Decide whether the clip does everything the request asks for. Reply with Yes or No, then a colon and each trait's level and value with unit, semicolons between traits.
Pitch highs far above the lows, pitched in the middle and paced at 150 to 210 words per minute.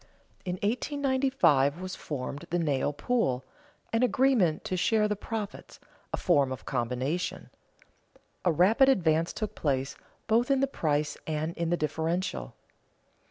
No: wide, 7.3 semitones; medium, 175 Hz; slow, 135 wpm